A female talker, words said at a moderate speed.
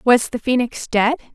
Yes: female; average, 180 wpm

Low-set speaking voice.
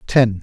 Yes: low, 115 Hz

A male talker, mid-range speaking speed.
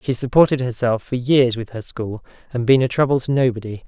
No: male; fast, 215 wpm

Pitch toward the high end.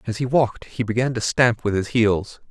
No: low, 115 Hz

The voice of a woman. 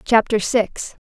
Yes: female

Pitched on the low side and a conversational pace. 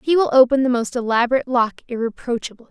No: high, 245 Hz; average, 175 wpm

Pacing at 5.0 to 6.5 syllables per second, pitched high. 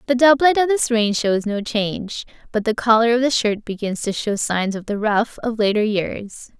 No: 4.8 syllables/s; high, 225 Hz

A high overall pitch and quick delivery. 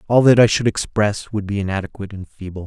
No: low, 105 Hz; fast, 225 wpm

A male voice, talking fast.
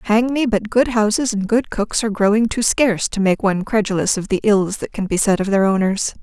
No: female; fast, 250 wpm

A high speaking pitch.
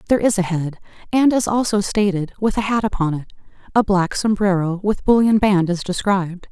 Yes: high, 195 Hz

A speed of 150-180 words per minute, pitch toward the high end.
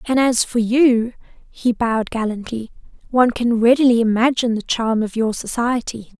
Yes: average, 155 wpm; high, 235 Hz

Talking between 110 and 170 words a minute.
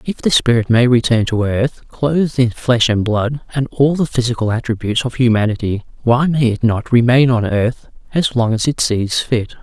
No: average, 200 wpm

